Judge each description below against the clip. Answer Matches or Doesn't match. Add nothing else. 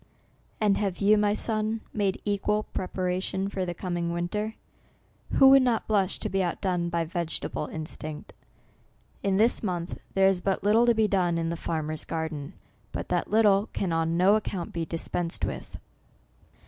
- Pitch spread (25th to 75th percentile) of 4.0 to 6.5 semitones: Doesn't match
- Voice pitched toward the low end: Doesn't match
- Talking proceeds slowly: Doesn't match